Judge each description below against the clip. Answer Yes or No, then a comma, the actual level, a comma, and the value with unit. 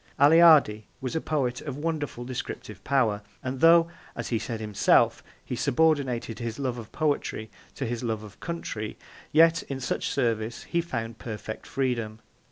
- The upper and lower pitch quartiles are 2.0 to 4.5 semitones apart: No, average, 5.1 semitones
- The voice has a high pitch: No, low, 125 Hz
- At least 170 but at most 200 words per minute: No, average, 160 wpm